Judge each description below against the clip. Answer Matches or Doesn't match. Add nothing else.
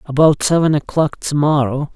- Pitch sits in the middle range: Matches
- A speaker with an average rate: Matches